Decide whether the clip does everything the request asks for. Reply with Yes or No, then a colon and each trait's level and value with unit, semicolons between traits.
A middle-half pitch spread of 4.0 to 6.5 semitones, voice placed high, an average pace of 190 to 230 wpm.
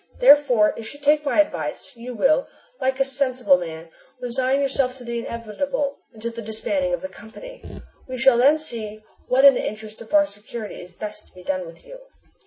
Yes: average, 4.5 semitones; high, 245 Hz; average, 195 wpm